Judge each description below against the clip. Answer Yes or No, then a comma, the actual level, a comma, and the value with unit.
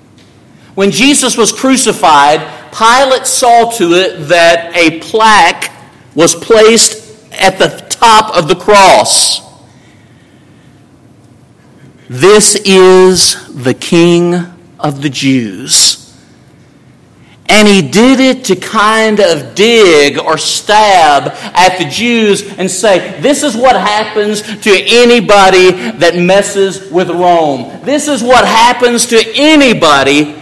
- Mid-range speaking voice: No, high, 195 Hz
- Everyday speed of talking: No, slow, 110 wpm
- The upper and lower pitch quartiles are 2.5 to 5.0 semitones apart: Yes, average, 4.7 semitones